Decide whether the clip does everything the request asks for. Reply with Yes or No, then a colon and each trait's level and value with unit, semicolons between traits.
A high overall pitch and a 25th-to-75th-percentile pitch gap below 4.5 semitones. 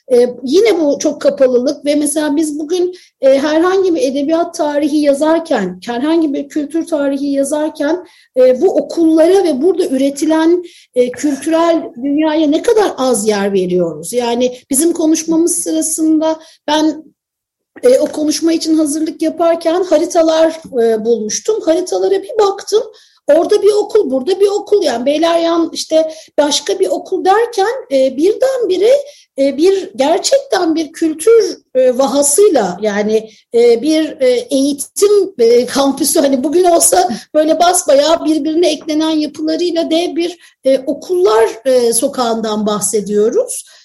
Yes: very high, 315 Hz; average, 4.1 semitones